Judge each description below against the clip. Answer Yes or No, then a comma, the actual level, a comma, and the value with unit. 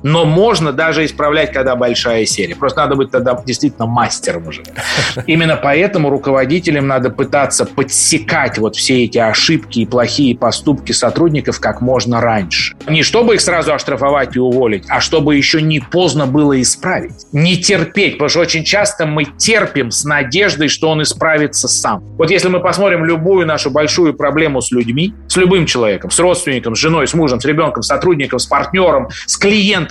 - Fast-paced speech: Yes, fast, 175 wpm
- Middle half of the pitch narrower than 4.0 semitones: No, average, 4.5 semitones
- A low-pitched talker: No, medium, 150 Hz